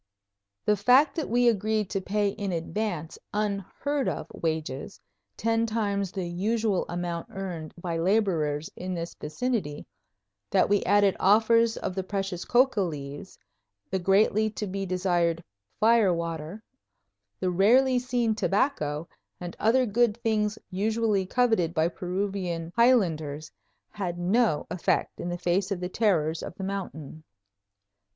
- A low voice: No, high, 195 Hz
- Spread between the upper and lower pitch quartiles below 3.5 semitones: No, average, 4.1 semitones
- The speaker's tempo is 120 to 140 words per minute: Yes, slow, 135 wpm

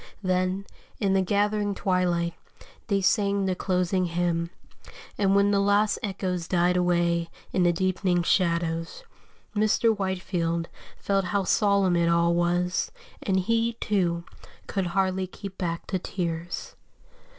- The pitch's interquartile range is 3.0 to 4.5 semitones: No, narrow, 2.4 semitones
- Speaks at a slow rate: Yes, slow, 130 wpm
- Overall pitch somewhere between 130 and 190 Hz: Yes, medium, 185 Hz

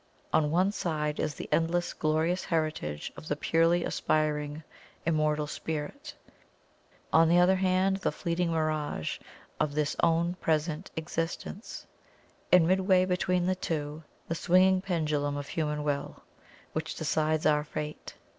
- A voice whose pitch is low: No, medium, 160 Hz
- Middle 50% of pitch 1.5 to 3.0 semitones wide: Yes, narrow, 2.5 semitones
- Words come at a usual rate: No, slow, 130 wpm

